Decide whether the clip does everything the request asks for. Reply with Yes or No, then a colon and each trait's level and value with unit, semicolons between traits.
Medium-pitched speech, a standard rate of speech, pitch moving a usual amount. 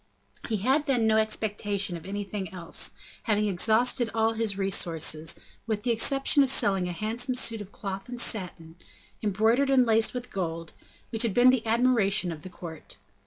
No: high, 215 Hz; average, 170 wpm; average, 3.8 semitones